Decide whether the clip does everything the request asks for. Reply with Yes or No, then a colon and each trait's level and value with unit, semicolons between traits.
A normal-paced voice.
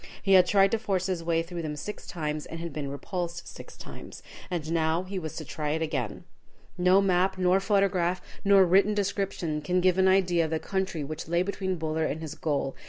No: fast, 215 wpm